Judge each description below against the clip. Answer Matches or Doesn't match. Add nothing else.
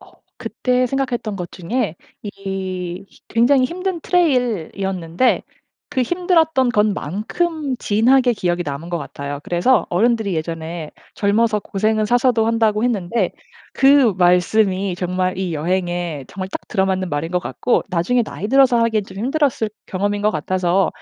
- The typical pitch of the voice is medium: Doesn't match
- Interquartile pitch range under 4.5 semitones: Doesn't match